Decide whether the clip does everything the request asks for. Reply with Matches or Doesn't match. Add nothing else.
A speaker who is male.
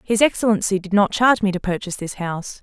Doesn't match